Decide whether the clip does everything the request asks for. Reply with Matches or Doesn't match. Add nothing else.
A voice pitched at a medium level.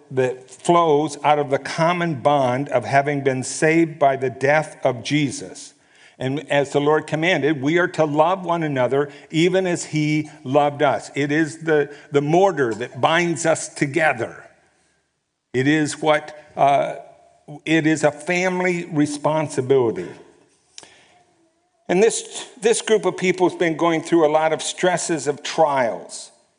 Matches